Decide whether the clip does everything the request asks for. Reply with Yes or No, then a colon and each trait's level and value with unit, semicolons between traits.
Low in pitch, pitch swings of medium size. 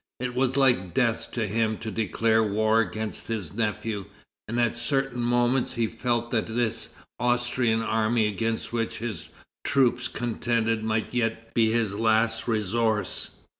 No: low, 115 Hz; narrow, 1.6 semitones